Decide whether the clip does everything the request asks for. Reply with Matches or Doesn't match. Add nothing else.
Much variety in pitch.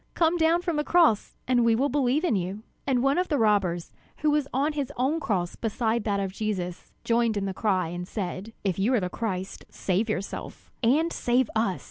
Matches